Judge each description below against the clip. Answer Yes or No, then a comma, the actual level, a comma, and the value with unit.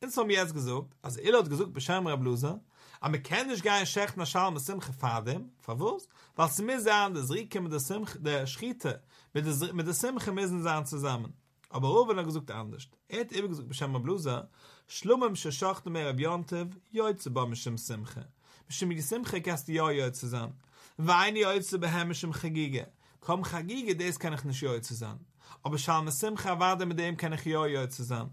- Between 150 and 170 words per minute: No, average, 190 wpm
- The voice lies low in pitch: No, medium, 160 Hz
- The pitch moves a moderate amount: No, wide, 5.7 semitones